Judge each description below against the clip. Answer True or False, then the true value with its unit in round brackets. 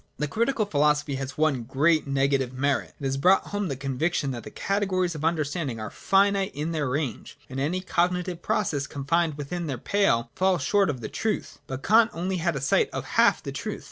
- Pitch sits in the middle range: True (155 Hz)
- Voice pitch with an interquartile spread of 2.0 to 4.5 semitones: False (5.1 semitones)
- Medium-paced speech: False (215 wpm)